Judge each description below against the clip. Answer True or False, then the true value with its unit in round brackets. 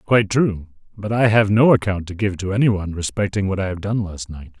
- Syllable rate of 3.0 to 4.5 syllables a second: False (5.6 syllables/s)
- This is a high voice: False (100 Hz)